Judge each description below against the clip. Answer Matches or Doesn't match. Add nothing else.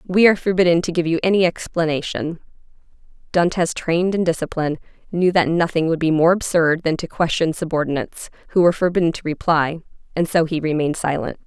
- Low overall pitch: Doesn't match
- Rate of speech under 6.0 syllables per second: Doesn't match